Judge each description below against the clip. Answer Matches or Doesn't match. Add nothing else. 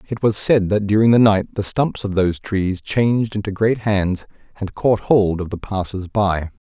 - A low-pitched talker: Matches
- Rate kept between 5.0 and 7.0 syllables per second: Doesn't match